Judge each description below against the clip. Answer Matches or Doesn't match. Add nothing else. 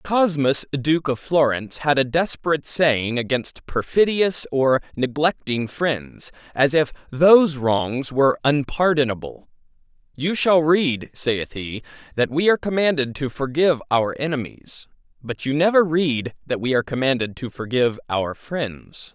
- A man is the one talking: Matches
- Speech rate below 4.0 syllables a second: Doesn't match